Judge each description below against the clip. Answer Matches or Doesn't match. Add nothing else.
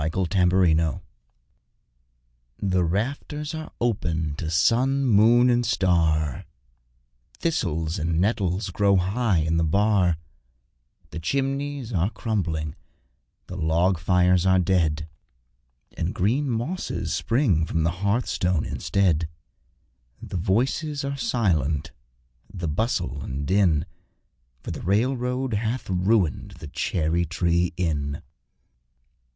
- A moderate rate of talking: Doesn't match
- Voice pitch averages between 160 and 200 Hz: Doesn't match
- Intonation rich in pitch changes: Matches